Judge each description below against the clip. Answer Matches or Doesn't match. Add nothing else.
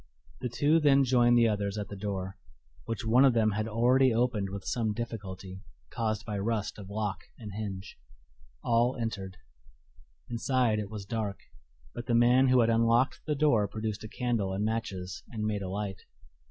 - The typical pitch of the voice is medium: Doesn't match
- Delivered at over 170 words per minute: Matches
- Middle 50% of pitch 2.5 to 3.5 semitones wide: Matches